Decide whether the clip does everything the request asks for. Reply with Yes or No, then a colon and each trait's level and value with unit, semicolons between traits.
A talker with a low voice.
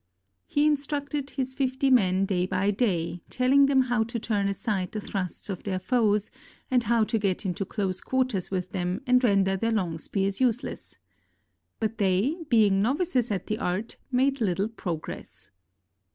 No: high, 215 Hz